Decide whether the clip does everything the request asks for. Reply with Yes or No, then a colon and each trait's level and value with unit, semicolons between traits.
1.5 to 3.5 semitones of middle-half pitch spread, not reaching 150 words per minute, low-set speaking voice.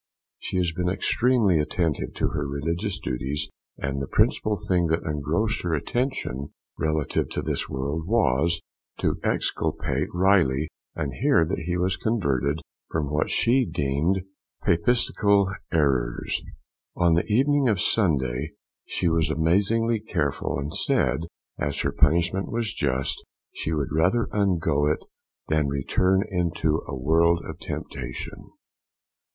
No: average, 5.0 semitones; slow, 135 wpm; very low, 80 Hz